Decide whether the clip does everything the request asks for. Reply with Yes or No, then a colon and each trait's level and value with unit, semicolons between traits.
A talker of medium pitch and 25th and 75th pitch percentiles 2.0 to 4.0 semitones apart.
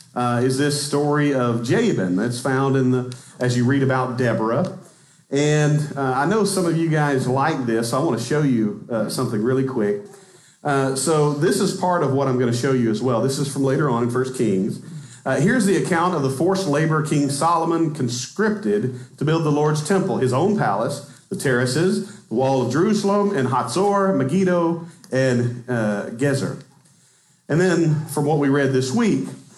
No: medium, 145 Hz; average, 4.4 semitones